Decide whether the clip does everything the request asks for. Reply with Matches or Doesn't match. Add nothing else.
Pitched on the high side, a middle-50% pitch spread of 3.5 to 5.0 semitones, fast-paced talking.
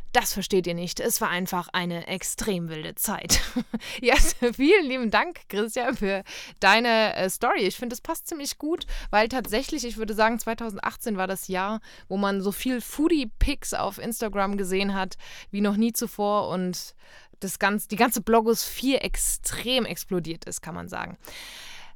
Doesn't match